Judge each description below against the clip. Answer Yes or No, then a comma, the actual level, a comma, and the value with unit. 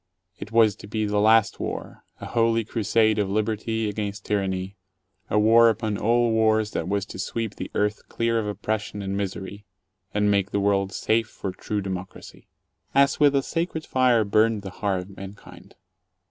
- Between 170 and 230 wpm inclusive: Yes, average, 175 wpm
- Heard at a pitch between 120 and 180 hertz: No, low, 105 Hz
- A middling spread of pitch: No, narrow, 2.1 semitones